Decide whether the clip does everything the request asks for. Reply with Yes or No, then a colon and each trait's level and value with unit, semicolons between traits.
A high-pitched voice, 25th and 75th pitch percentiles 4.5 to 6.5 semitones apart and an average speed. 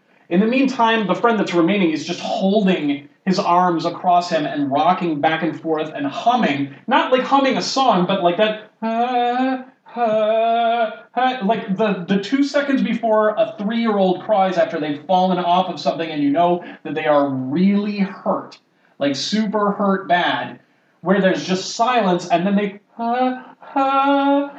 Yes: high, 200 Hz; average, 5.2 semitones; average, 170 wpm